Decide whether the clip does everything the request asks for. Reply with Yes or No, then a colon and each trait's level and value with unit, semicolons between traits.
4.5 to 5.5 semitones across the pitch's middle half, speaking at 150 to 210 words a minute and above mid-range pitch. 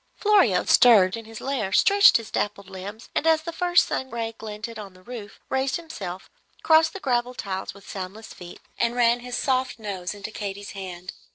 Yes: average, 4.9 semitones; average, 190 wpm; high, 225 Hz